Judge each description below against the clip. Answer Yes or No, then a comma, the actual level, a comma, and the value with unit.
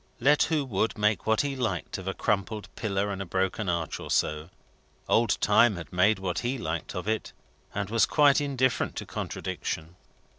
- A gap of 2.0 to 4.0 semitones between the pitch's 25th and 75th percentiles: No, average, 4.6 semitones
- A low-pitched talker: Yes, low, 105 Hz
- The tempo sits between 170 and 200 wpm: Yes, average, 185 wpm